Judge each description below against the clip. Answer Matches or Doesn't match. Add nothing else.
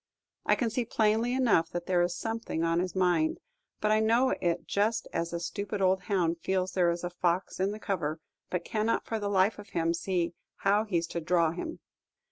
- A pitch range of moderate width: Matches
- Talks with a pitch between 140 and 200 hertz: Matches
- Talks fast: Matches